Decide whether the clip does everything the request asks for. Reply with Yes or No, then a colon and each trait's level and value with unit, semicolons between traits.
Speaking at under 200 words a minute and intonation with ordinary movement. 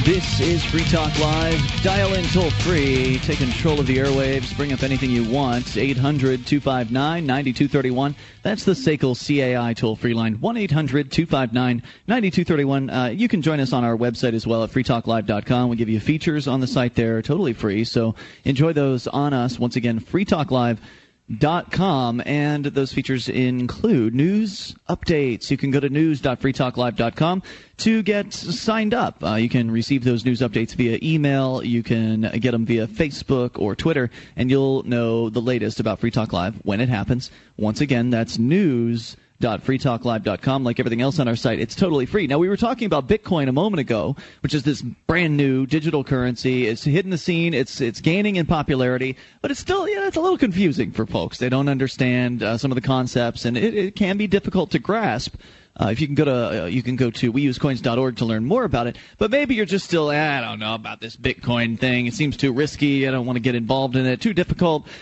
No: fast, 205 wpm; average, 4.2 semitones